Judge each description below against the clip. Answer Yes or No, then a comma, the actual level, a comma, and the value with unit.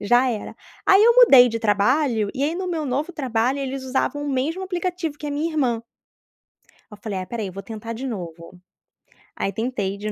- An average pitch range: No, wide, 5.7 semitones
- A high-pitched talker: Yes, very high, 255 Hz